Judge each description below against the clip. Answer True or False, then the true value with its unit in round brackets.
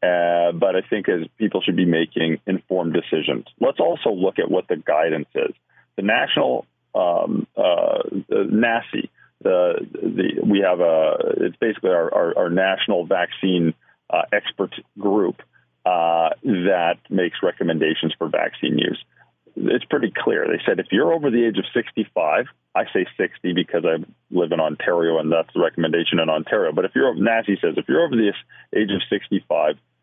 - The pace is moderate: True (170 wpm)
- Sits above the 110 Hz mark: False (90 Hz)